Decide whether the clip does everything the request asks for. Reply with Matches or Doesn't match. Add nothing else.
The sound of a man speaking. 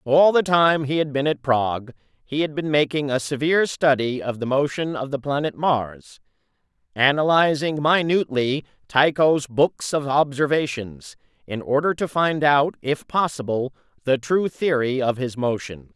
Matches